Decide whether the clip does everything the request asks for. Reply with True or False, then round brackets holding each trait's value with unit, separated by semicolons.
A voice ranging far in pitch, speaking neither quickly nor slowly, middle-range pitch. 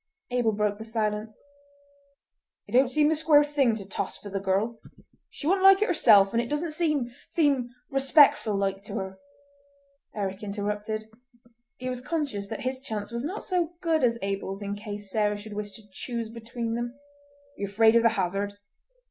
False (5.7 semitones; 180 wpm; 230 Hz)